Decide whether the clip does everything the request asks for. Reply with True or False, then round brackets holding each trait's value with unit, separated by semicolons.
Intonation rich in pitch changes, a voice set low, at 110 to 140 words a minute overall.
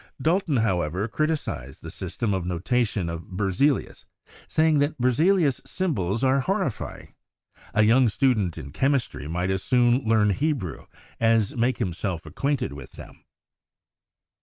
True (7.0 semitones; 115 Hz; 135 wpm)